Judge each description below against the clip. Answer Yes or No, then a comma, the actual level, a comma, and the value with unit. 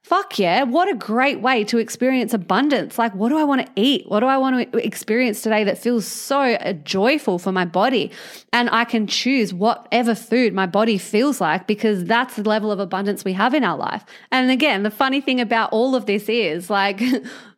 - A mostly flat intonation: No, average, 3.7 semitones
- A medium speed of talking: No, fast, 210 wpm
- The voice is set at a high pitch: Yes, high, 230 Hz